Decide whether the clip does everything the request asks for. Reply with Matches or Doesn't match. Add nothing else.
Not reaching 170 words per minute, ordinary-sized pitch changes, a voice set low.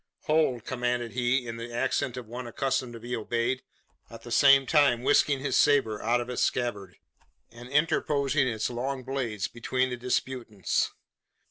Doesn't match